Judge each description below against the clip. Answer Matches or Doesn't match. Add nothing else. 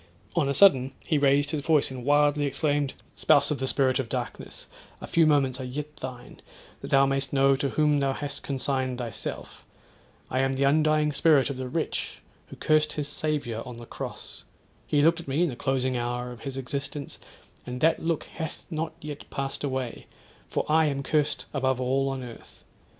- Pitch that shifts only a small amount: Matches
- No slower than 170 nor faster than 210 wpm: Matches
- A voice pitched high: Doesn't match